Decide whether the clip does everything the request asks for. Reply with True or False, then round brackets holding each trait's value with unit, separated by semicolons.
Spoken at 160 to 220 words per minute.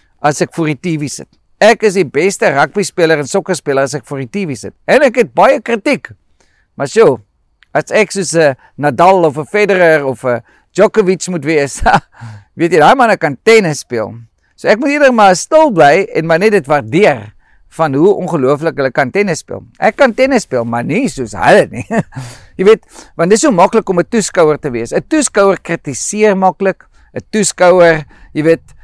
True (190 wpm)